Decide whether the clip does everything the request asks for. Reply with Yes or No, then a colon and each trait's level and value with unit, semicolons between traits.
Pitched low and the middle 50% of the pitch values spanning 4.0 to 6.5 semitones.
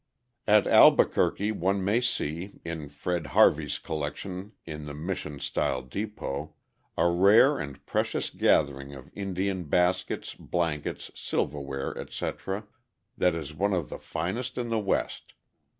Yes: very low, 85 Hz; average, 5.1 semitones